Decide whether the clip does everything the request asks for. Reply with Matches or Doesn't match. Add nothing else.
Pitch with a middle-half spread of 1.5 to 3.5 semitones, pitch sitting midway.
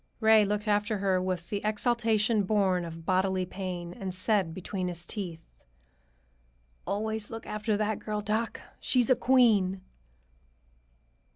Doesn't match